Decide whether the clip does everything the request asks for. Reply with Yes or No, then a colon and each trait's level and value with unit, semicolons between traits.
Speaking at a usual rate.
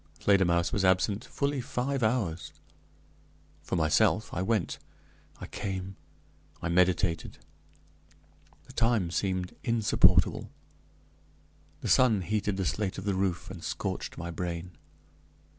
No: slow, 115 wpm